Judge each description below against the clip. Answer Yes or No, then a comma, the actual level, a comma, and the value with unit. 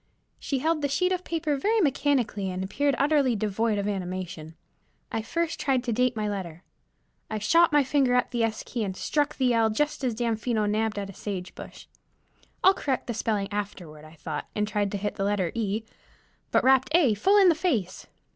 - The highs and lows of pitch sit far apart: Yes, wide, 5.8 semitones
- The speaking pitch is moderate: No, high, 225 Hz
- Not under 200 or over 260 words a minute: Yes, fast, 205 wpm